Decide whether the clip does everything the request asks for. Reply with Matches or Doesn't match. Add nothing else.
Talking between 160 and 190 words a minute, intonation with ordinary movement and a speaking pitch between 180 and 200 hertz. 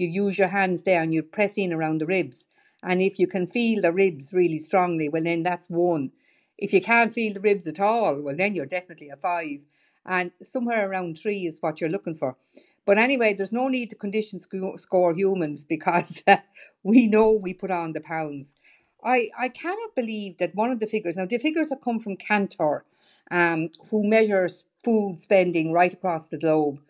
Doesn't match